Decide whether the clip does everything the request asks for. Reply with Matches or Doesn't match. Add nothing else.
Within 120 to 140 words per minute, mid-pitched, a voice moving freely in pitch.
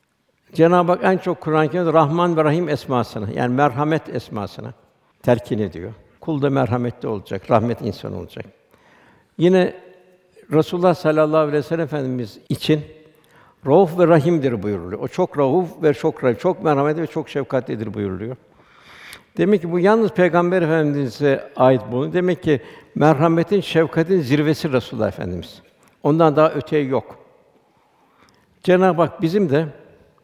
Doesn't match